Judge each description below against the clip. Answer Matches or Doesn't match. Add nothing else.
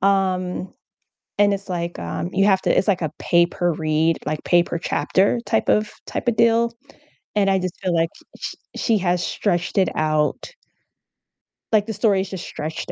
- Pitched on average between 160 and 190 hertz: Matches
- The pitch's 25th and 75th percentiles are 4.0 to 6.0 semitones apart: Doesn't match